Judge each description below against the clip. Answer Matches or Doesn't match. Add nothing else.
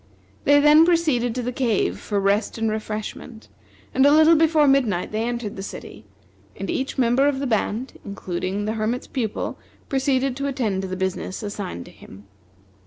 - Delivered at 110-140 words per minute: Doesn't match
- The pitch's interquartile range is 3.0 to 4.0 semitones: Doesn't match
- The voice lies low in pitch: Doesn't match